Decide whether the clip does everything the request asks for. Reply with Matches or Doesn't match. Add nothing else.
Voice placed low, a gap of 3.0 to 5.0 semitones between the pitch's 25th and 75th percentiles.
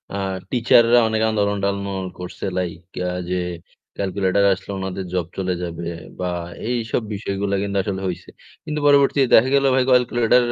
Matches